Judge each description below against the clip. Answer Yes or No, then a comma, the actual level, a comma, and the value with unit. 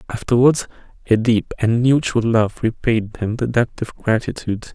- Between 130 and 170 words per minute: Yes, average, 150 wpm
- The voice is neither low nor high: No, low, 115 Hz